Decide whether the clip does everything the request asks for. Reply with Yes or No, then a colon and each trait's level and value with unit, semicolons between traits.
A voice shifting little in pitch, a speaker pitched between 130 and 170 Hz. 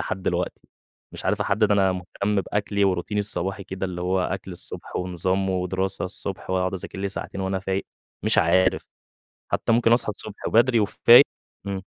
No: narrow, 1.7 semitones; very low, 95 Hz